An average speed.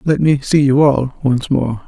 No: fast, 225 wpm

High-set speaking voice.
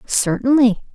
Yes: high, 240 Hz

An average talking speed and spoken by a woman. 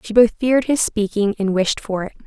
No: fast, 240 wpm; female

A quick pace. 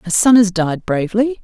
Yes: fast, 210 wpm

